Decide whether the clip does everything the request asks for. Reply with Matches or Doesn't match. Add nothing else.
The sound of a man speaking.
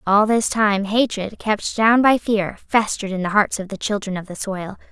Doesn't match